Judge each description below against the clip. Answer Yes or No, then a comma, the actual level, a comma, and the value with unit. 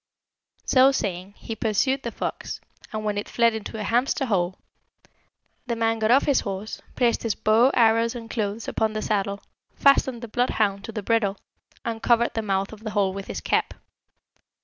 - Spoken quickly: No, average, 185 wpm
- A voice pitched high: Yes, high, 220 Hz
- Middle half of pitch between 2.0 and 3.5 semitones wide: Yes, narrow, 2.5 semitones